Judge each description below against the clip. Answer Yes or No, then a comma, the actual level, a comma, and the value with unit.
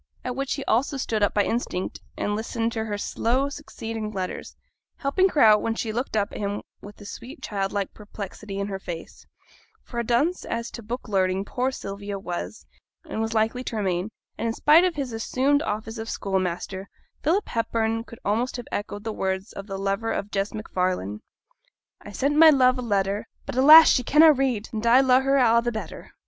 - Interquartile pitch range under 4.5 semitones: Yes, average, 4.1 semitones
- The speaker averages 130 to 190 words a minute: No, average, 200 wpm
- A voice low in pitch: No, high, 225 Hz